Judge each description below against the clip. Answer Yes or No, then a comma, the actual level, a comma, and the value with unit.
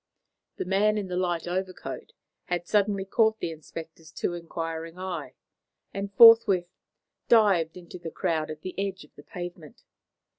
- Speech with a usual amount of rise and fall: Yes, average, 3.2 semitones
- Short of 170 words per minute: Yes, average, 150 wpm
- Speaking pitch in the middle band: Yes, medium, 180 Hz